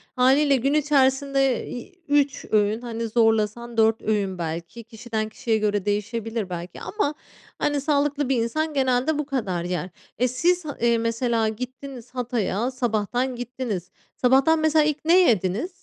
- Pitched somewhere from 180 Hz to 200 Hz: No, high, 245 Hz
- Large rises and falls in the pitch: No, average, 4.2 semitones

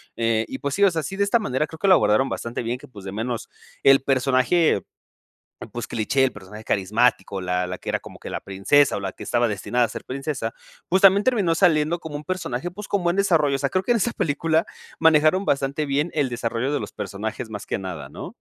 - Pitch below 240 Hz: Yes, low, 135 Hz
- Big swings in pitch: Yes, wide, 6.8 semitones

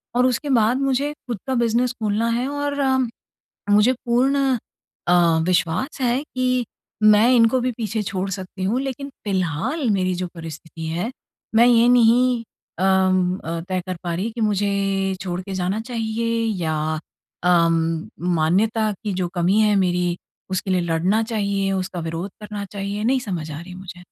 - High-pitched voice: Yes, high, 205 Hz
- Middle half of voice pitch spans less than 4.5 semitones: No, average, 4.8 semitones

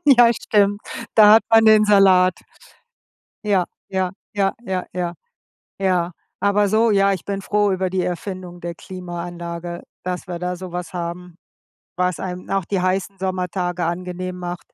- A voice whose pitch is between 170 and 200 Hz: Yes, medium, 185 Hz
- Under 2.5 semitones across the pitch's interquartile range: Yes, narrow, 1.9 semitones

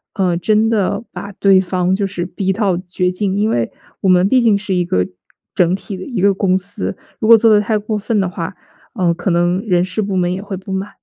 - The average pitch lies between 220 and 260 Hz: No, high, 190 Hz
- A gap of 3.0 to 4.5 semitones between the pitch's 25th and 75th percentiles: No, narrow, 2.4 semitones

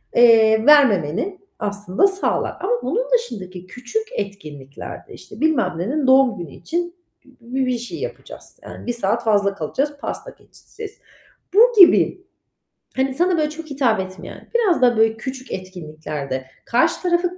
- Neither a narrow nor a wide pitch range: No, wide, 8.6 semitones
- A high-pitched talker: Yes, high, 245 Hz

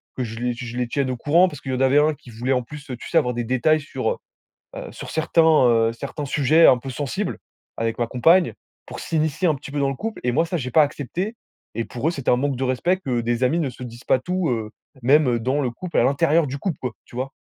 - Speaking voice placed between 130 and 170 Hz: Yes, low, 135 Hz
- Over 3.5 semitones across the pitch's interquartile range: Yes, average, 4.1 semitones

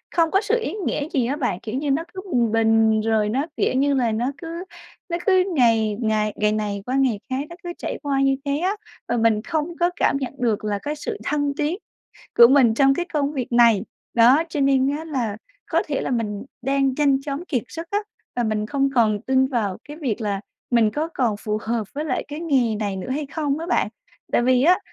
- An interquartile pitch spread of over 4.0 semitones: Yes, average, 4.9 semitones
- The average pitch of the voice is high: Yes, very high, 265 Hz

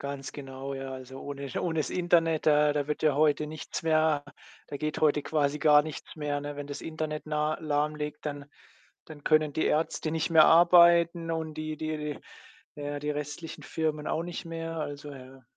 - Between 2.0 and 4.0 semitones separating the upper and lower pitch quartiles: No, narrow, 1.6 semitones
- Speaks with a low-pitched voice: No, medium, 150 Hz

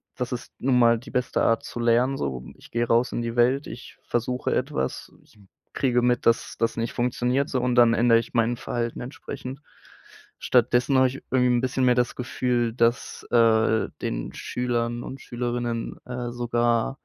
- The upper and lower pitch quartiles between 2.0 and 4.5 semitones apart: No, narrow, 1.2 semitones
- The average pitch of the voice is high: No, low, 120 Hz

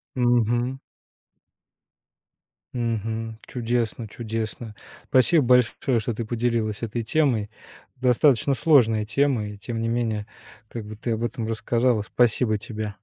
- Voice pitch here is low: Yes, low, 115 Hz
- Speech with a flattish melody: Yes, narrow, 2.0 semitones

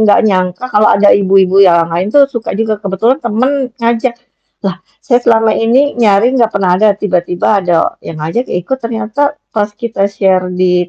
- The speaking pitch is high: Yes, high, 210 Hz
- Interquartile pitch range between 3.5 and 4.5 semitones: Yes, average, 4.0 semitones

